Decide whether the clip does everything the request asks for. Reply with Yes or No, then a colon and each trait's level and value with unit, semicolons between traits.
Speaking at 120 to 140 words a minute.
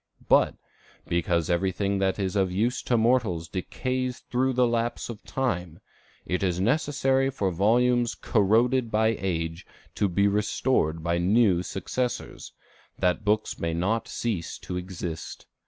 Yes: slow, 135 wpm